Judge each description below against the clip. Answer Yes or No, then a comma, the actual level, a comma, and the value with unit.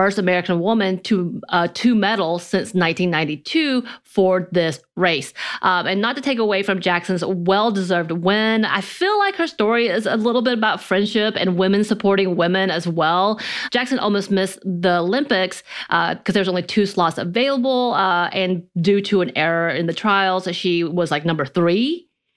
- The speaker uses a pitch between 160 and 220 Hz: Yes, high, 190 Hz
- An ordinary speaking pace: Yes, average, 175 wpm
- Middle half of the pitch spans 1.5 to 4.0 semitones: Yes, average, 3.6 semitones